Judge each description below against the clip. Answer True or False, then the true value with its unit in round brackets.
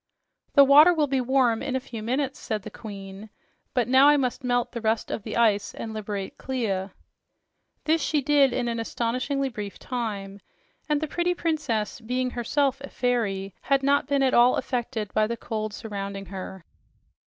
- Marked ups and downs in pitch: False (4.2 semitones)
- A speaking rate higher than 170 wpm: True (180 wpm)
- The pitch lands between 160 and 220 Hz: False (240 Hz)